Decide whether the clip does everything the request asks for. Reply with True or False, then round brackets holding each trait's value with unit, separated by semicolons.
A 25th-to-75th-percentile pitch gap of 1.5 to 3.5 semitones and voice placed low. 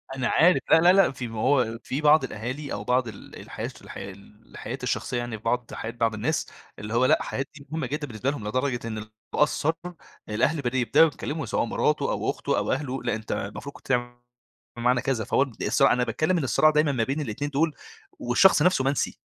False (4.2 semitones; 130 Hz)